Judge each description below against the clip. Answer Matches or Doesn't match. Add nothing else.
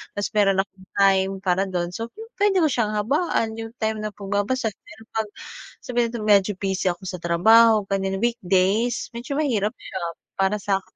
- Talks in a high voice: Matches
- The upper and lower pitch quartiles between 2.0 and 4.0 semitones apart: Matches